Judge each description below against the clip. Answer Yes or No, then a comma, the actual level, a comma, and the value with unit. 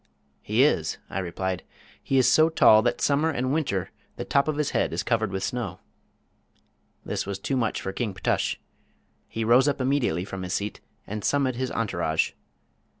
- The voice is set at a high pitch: No, low, 115 Hz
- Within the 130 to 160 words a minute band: No, average, 180 wpm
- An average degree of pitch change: No, wide, 5.9 semitones